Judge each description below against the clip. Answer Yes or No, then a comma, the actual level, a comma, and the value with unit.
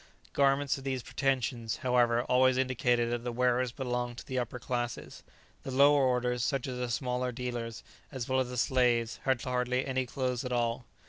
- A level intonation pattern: Yes, narrow, 1.3 semitones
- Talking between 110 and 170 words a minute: No, average, 185 wpm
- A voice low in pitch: Yes, low, 125 Hz